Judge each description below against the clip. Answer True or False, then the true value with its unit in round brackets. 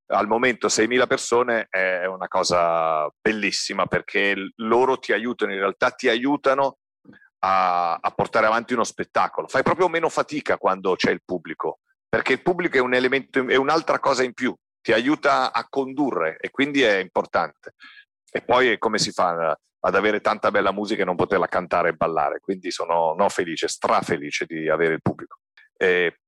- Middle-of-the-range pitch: False (130 Hz)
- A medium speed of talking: False (175 wpm)